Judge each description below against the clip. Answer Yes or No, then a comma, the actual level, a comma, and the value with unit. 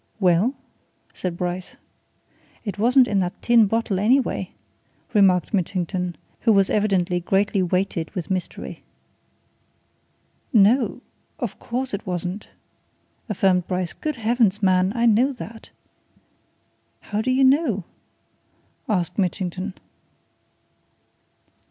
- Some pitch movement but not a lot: Yes, average, 4.0 semitones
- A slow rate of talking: Yes, slow, 105 wpm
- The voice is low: No, high, 200 Hz